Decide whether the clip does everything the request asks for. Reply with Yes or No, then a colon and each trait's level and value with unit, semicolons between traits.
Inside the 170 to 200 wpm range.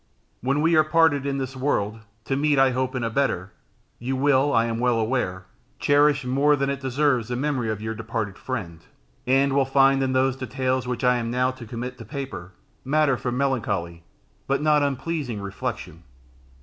Yes: average, 190 wpm